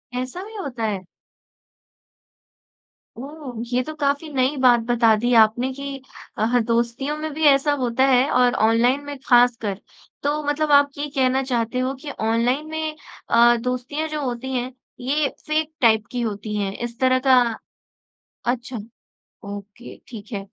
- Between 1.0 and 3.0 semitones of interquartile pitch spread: No, average, 3.4 semitones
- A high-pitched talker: Yes, very high, 255 Hz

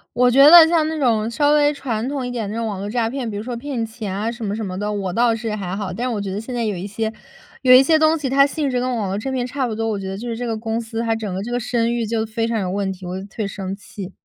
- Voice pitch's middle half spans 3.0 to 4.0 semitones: Yes, average, 3.4 semitones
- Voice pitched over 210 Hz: Yes, high, 225 Hz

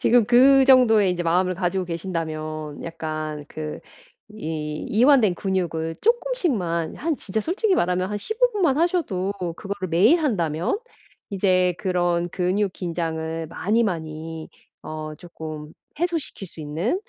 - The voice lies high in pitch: No, medium, 180 Hz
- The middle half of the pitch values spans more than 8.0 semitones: No, wide, 5.6 semitones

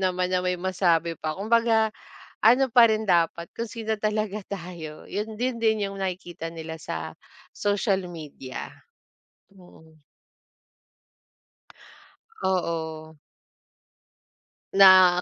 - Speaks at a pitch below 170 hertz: No, medium, 185 Hz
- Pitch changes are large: No, average, 4.3 semitones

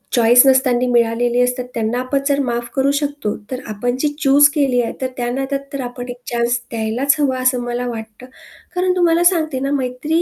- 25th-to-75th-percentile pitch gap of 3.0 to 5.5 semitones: No, narrow, 2.6 semitones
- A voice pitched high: Yes, very high, 250 Hz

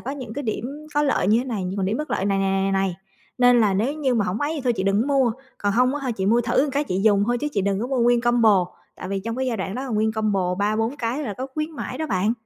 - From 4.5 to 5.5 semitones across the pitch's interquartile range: Yes, average, 4.8 semitones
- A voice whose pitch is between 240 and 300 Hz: No, high, 230 Hz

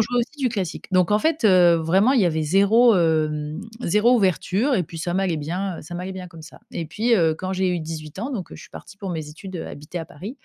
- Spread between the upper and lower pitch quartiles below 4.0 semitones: No, average, 4.4 semitones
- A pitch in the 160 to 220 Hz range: Yes, medium, 185 Hz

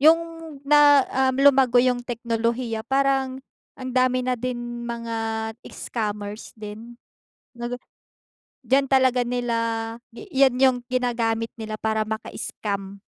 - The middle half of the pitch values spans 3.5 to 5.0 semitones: No, narrow, 2.4 semitones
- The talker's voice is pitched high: Yes, high, 240 Hz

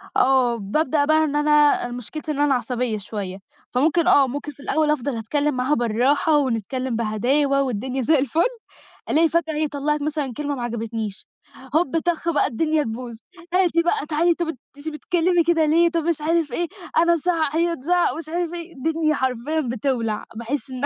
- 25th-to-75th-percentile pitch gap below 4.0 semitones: No, average, 4.3 semitones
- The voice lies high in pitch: Yes, very high, 290 Hz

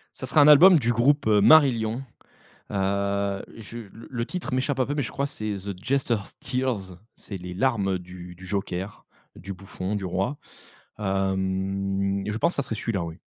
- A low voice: Yes, low, 100 Hz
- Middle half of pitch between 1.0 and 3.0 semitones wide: No, average, 5.0 semitones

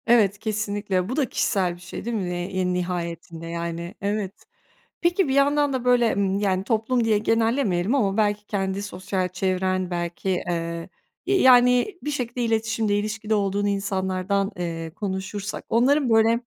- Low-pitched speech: No, high, 205 Hz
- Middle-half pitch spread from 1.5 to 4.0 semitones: Yes, average, 3.7 semitones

